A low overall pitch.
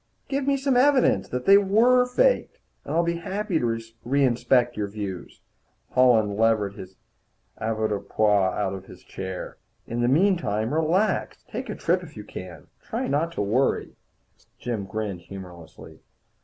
Yes: low, 120 Hz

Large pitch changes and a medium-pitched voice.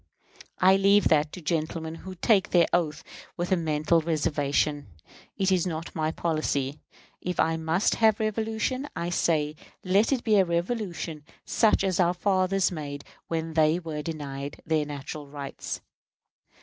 No: average, 3.6 semitones; medium, 165 Hz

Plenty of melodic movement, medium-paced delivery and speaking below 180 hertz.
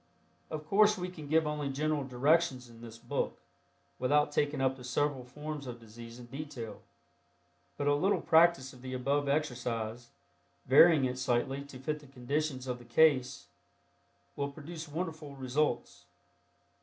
No: average, 3.4 semitones; average, 155 wpm; medium, 140 Hz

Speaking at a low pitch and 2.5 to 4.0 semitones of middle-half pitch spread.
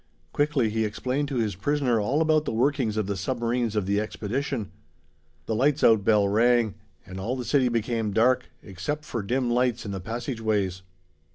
Yes: low, 115 Hz; average, 3.5 semitones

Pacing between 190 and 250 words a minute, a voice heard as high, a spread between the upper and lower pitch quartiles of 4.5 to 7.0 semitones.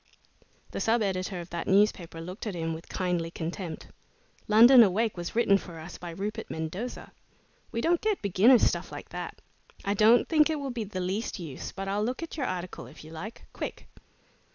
Yes: average, 195 wpm; high, 195 Hz; average, 4.9 semitones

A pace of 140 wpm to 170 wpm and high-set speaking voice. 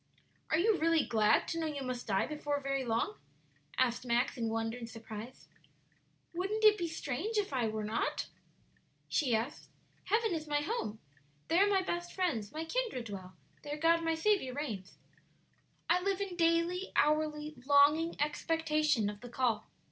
Yes: average, 165 wpm; very high, 300 Hz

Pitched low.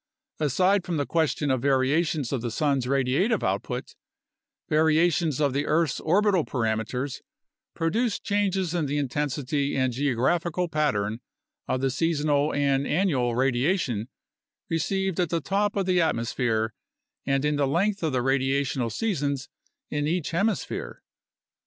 No: medium, 145 Hz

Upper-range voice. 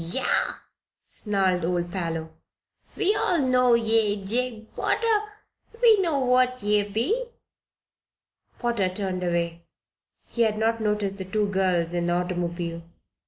Yes: high, 205 Hz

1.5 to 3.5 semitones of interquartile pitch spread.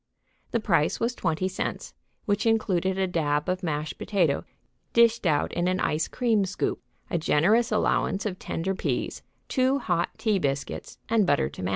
No: average, 5.1 semitones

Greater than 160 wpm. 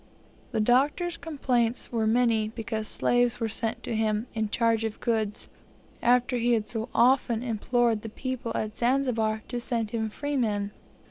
No: average, 155 wpm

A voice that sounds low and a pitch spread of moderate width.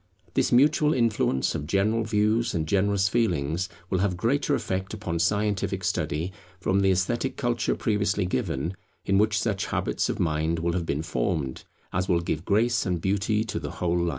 Yes: very low, 95 Hz; average, 4.1 semitones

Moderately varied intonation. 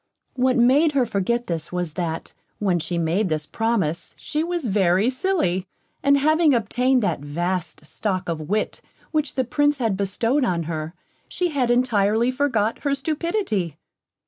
No: wide, 7.4 semitones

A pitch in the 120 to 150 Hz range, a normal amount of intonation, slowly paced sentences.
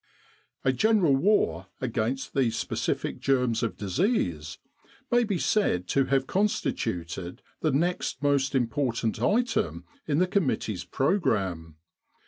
No: low, 135 Hz; wide, 8.8 semitones; slow, 120 wpm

